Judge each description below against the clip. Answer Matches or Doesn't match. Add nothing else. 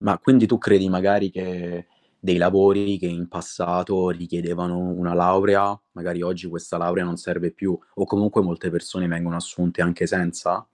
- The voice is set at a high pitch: Doesn't match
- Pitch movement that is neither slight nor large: Doesn't match